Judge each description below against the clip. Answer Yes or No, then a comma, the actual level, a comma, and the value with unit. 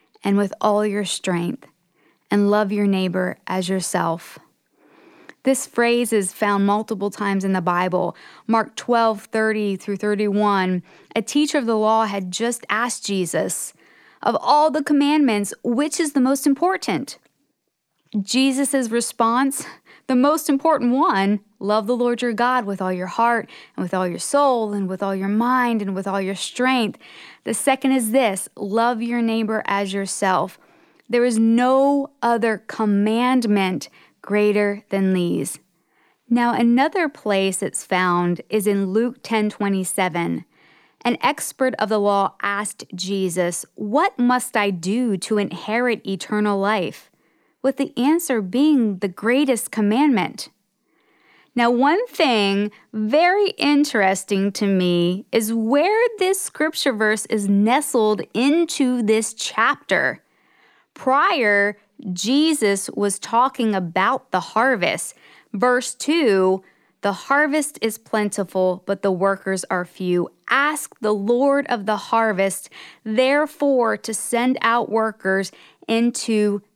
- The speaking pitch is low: No, high, 220 Hz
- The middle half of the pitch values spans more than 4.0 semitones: Yes, average, 4.4 semitones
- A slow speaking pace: Yes, slow, 130 wpm